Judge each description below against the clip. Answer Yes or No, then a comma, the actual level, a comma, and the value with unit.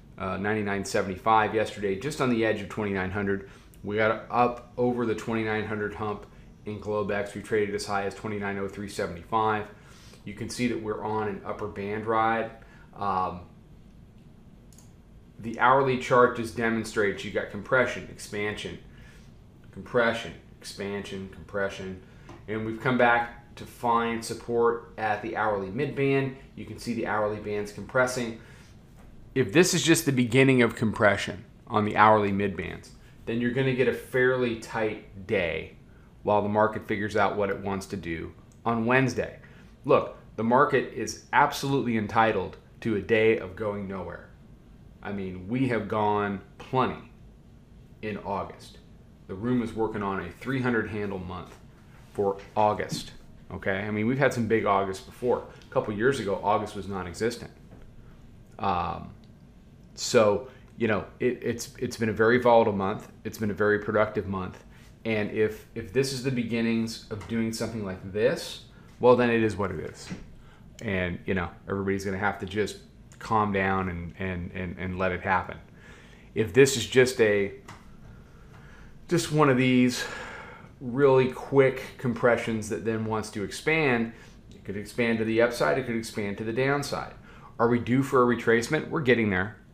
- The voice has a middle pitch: No, low, 110 Hz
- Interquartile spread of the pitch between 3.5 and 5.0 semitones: No, average, 3.0 semitones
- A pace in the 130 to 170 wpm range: Yes, average, 160 wpm